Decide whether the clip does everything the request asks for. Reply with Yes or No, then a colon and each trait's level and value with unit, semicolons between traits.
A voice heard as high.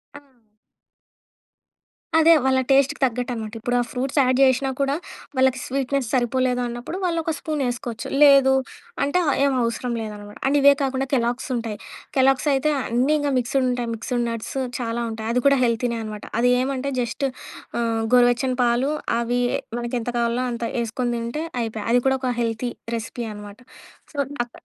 Yes: very high, 250 Hz